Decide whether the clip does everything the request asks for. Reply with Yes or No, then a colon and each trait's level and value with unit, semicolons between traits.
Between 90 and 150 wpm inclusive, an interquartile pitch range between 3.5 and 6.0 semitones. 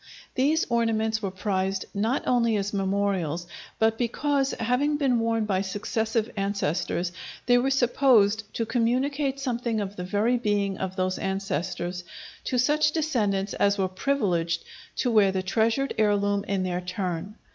Yes: average, 145 wpm; average, 4.2 semitones